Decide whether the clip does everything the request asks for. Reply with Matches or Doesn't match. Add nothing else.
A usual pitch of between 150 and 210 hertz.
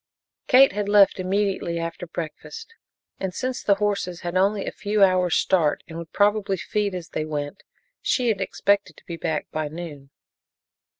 Matches